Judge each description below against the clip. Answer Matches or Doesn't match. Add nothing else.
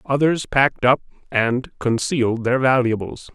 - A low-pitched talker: Matches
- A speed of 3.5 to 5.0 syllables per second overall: Matches